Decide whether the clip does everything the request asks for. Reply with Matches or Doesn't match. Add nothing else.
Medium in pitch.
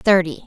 Matches